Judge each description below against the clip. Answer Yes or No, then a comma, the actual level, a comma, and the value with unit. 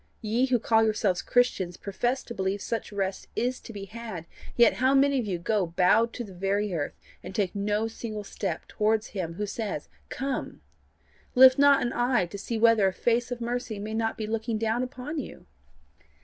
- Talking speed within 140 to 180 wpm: No, average, 195 wpm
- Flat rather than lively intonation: No, average, 3.3 semitones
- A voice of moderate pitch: No, high, 220 Hz